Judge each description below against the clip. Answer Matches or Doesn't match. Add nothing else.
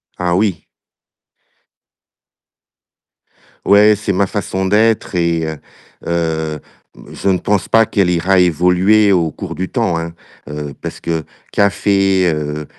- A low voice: Matches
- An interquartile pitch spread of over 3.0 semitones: Matches